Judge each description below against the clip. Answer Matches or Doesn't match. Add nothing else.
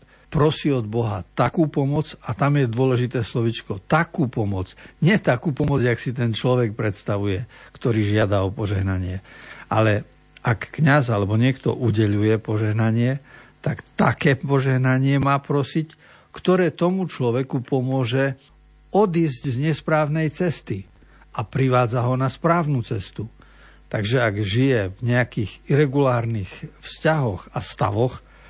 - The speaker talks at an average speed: Matches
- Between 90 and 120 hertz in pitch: Doesn't match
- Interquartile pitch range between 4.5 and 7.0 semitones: Matches